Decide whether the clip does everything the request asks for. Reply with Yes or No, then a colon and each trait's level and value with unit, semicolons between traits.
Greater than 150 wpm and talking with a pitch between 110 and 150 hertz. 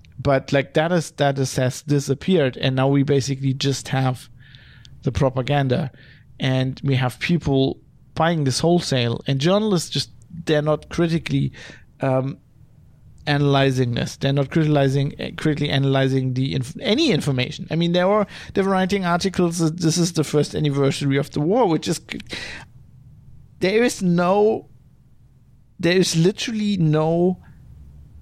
No: average, 140 wpm; medium, 140 Hz